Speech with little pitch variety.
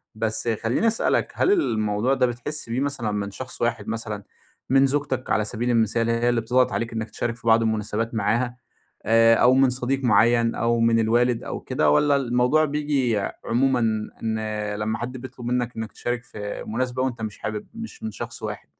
Yes: narrow, 2.3 semitones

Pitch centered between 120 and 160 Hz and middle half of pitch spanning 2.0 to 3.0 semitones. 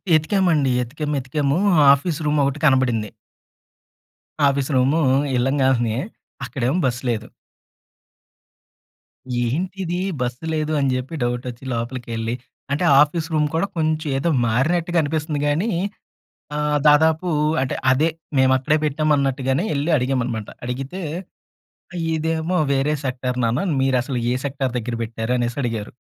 No: low, 135 Hz; average, 3.7 semitones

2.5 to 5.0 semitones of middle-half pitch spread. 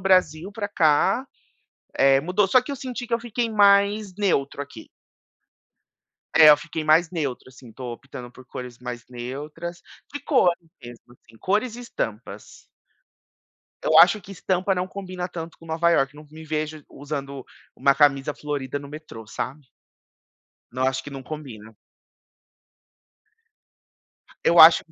No: wide, 5.6 semitones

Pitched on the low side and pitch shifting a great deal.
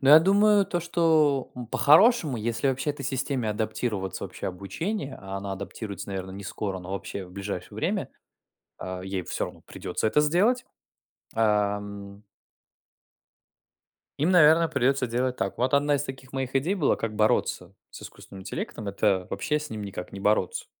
Yes: low, 120 Hz; wide, 6.8 semitones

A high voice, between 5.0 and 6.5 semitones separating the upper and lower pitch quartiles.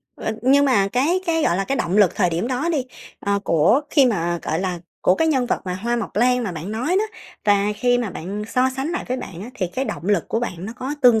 Yes: high, 230 Hz; wide, 5.4 semitones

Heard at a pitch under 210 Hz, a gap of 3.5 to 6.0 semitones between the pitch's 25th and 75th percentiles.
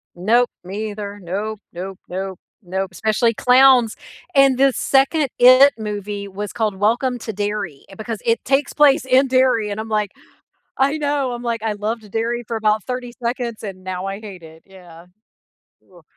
No: high, 220 Hz; average, 4.0 semitones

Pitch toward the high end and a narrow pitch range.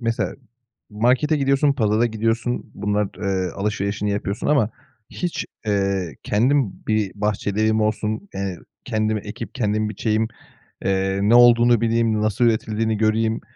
No: low, 110 Hz; narrow, 2.1 semitones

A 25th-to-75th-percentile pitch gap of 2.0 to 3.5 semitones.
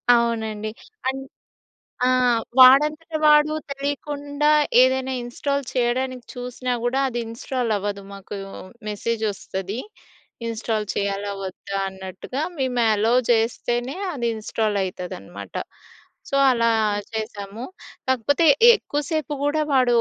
No: average, 4.1 semitones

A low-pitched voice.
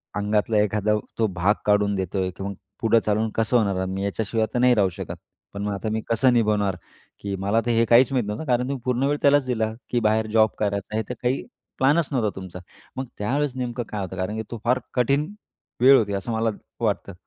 Yes: low, 110 Hz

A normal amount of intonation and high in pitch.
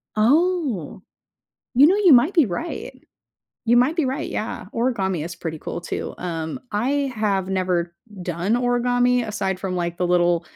No: wide, 6.2 semitones; high, 215 Hz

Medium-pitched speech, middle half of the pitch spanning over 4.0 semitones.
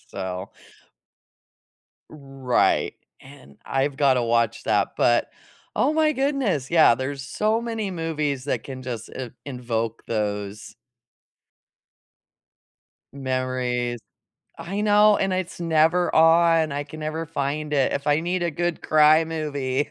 Yes: medium, 145 Hz; average, 4.7 semitones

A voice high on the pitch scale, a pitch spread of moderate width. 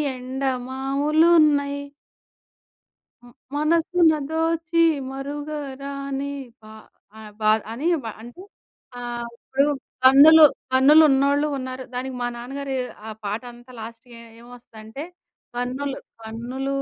Yes: very high, 270 Hz; average, 3.0 semitones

